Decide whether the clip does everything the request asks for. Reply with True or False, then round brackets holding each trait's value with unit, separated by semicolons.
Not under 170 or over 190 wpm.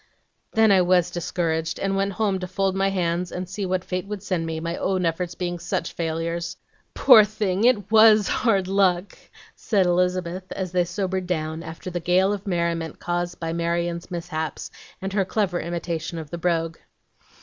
True (180 wpm)